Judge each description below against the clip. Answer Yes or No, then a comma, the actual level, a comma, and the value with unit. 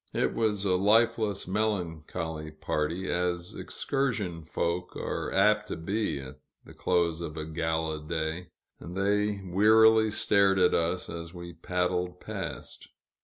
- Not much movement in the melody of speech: No, average, 3.8 semitones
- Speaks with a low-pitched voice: Yes, very low, 90 Hz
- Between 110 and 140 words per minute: Yes, slow, 135 wpm